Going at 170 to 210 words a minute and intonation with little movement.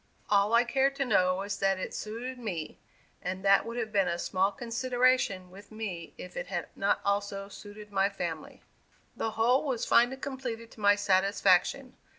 No: average, 175 wpm; average, 3.7 semitones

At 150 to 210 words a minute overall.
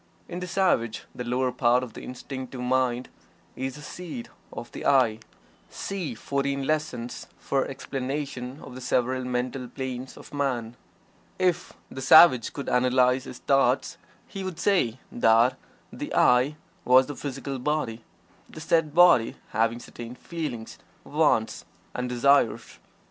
No: average, 140 wpm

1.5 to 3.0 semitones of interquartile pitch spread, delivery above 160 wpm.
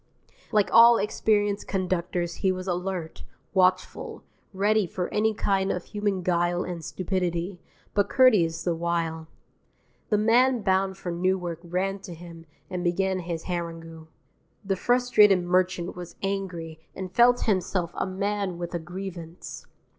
No: narrow, 2.4 semitones; average, 140 wpm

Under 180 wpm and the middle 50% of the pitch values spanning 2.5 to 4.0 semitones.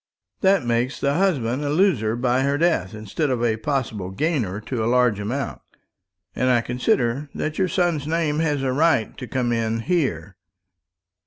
No: average, 170 wpm; average, 4.8 semitones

